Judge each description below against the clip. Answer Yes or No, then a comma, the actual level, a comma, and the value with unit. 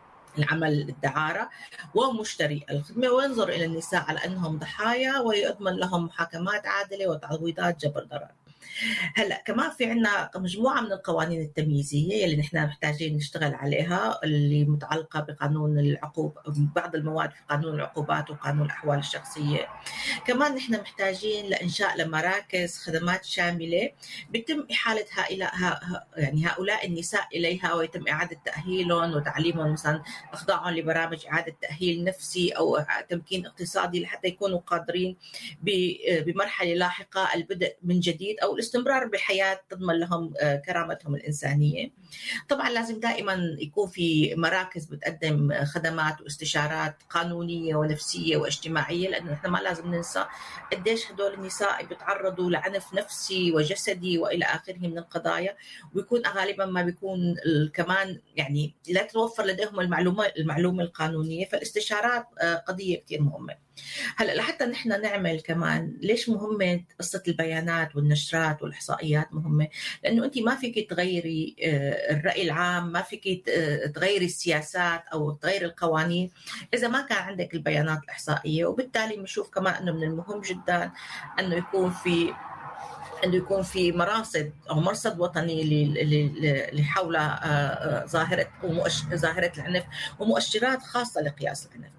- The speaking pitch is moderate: Yes, medium, 175 Hz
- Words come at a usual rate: Yes, average, 125 wpm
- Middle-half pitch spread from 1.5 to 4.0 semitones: Yes, average, 3.7 semitones